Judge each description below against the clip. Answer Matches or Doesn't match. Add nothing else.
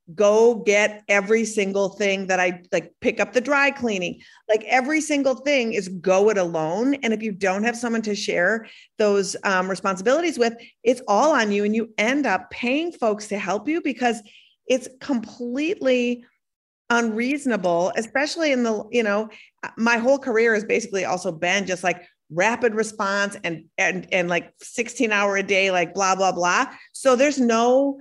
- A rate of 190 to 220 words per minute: Doesn't match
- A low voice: Doesn't match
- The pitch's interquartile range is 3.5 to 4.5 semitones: Matches